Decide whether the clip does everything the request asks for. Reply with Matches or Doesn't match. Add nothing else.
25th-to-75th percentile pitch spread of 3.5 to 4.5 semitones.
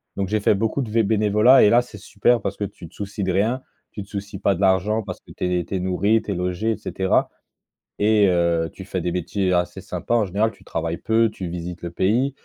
Doesn't match